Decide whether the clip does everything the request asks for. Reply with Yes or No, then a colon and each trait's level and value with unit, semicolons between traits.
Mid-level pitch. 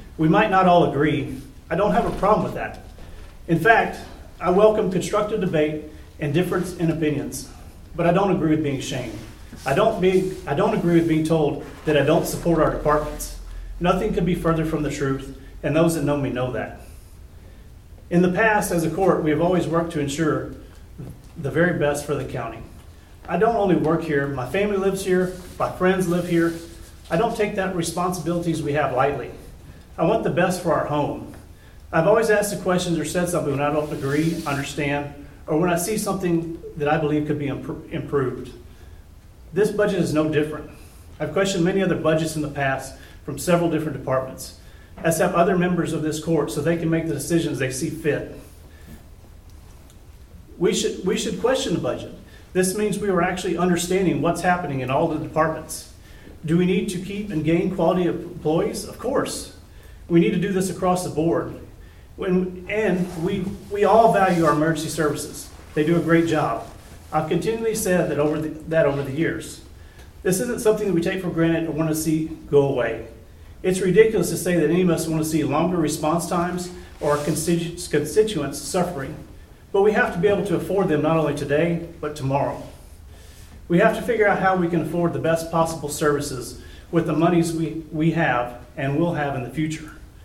Yes: medium, 160 Hz